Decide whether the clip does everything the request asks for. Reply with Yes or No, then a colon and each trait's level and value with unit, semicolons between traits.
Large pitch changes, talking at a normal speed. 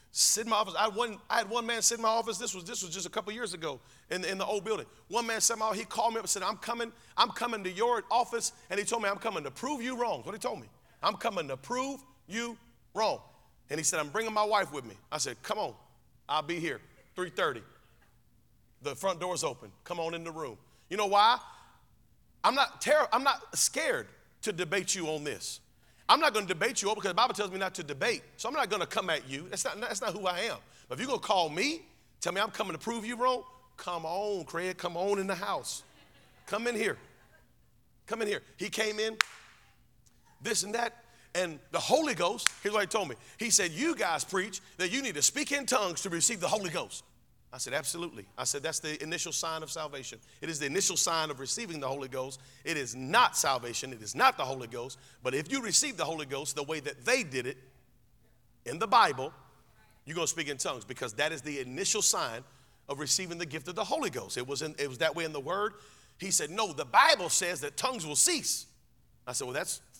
No: wide, 6.5 semitones; fast, 250 wpm